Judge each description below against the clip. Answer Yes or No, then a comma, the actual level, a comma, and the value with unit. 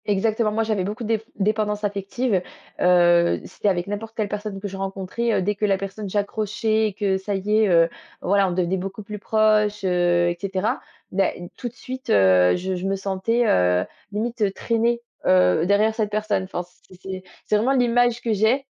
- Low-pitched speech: No, high, 205 Hz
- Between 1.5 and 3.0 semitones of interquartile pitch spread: Yes, narrow, 2.6 semitones